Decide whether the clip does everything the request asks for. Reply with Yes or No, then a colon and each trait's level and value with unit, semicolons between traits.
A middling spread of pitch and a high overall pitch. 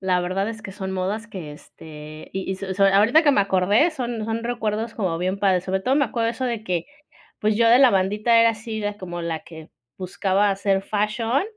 Yes: average, 3.4 semitones; high, 205 Hz